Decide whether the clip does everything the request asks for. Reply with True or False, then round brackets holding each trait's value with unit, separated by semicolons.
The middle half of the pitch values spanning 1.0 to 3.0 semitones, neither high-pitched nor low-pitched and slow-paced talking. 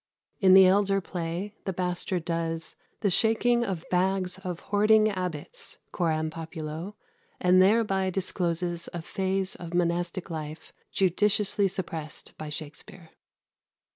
True (2.7 semitones; 180 Hz; 120 wpm)